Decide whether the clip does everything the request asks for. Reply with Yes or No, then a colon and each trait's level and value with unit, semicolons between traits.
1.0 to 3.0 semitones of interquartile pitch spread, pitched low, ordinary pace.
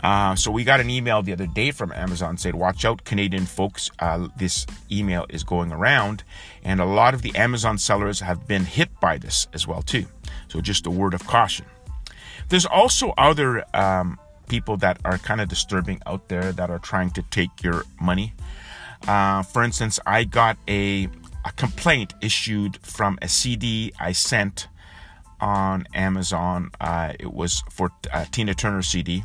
Yes: narrow, 2.6 semitones; very low, 95 Hz; average, 175 wpm